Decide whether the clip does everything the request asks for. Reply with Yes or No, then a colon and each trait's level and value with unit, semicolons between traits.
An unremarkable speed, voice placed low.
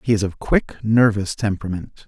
Yes: average, 175 wpm; low, 100 Hz